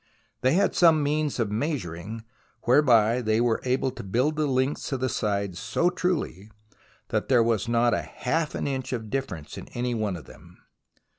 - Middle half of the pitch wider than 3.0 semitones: Yes, average, 4.7 semitones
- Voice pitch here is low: Yes, low, 120 Hz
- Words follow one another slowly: No, average, 175 wpm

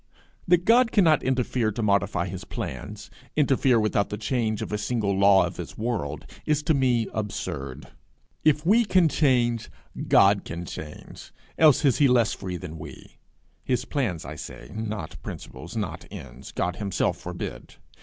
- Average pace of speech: Yes, average, 160 wpm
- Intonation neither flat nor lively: No, wide, 5.8 semitones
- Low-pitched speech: Yes, low, 110 Hz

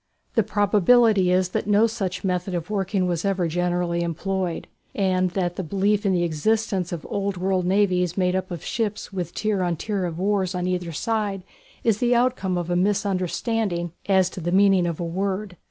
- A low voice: No, medium, 185 Hz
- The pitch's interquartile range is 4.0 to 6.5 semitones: No, narrow, 2.4 semitones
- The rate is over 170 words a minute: Yes, average, 190 wpm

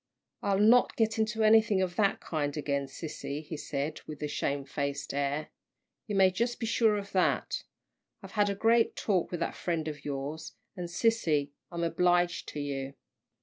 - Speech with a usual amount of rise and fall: No, wide, 6.1 semitones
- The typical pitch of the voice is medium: Yes, medium, 170 Hz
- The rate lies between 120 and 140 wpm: No, average, 175 wpm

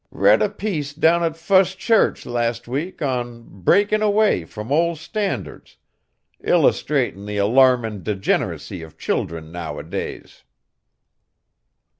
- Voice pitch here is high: No, low, 130 Hz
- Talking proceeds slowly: Yes, slow, 110 wpm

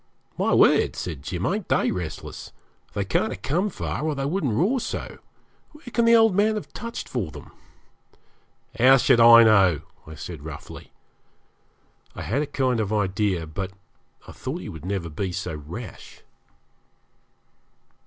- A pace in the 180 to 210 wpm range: No, average, 160 wpm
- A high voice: No, low, 110 Hz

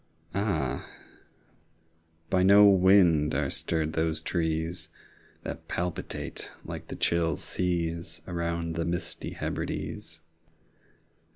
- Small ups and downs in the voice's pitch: Yes, narrow, 1.9 semitones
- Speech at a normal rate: No, slow, 100 wpm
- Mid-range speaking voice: No, very low, 85 Hz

